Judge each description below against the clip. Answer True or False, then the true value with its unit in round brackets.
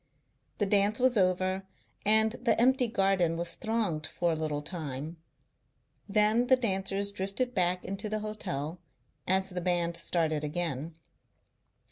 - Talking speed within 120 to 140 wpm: True (135 wpm)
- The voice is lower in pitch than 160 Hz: False (190 Hz)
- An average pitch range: True (4.1 semitones)